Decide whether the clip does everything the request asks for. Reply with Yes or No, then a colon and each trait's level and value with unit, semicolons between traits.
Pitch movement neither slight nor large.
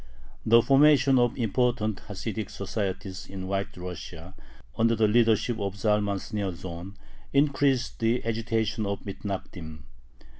Yes: average, 3.3 semitones